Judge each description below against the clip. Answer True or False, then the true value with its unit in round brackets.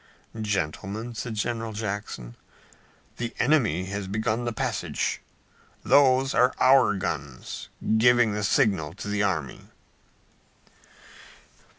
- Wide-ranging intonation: False (4.0 semitones)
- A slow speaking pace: True (100 wpm)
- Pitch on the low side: True (105 Hz)